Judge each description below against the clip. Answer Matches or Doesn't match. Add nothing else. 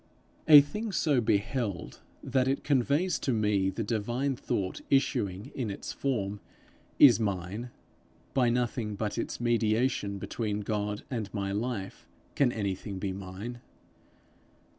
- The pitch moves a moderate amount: Matches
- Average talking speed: Doesn't match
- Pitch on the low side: Matches